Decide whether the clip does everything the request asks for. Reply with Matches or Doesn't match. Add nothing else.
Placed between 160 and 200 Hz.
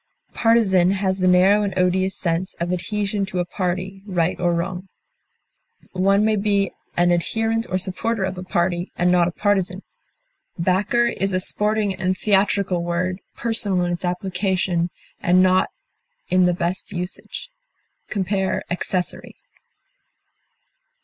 Matches